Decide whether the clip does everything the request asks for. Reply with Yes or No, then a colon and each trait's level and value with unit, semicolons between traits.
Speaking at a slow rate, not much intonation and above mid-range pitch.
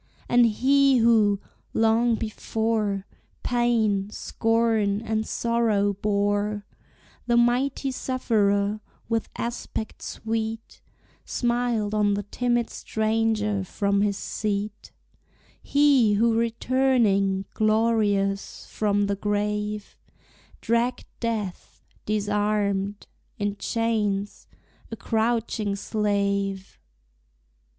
Yes: slow, 85 wpm; narrow, 2.3 semitones; high, 215 Hz